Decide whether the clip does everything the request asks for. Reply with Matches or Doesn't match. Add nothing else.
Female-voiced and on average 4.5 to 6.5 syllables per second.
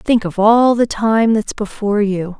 Doesn't match